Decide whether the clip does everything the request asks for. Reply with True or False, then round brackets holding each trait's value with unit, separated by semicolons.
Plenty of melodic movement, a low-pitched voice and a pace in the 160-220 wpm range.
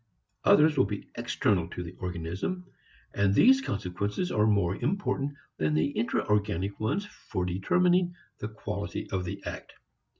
False (8.5 semitones; 105 Hz; 145 wpm)